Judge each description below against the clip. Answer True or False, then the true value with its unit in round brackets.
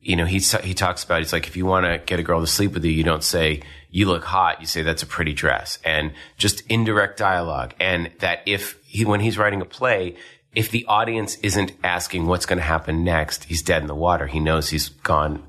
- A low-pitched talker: True (90 Hz)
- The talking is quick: True (245 wpm)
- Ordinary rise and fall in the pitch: True (3.9 semitones)